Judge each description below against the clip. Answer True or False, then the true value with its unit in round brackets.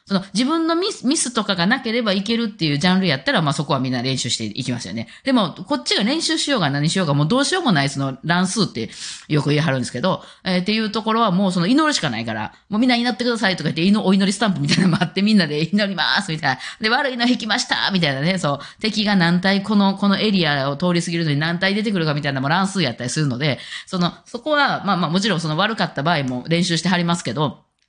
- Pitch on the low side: False (185 Hz)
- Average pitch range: False (6.2 semitones)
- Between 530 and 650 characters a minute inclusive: True (535 characters per minute)